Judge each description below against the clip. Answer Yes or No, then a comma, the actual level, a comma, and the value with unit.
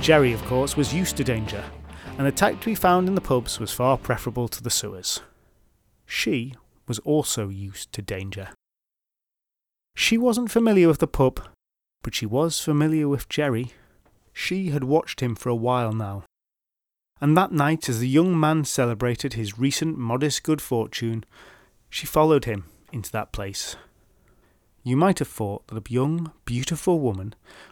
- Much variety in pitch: Yes, wide, 5.9 semitones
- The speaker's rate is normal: Yes, average, 165 wpm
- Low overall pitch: Yes, low, 125 Hz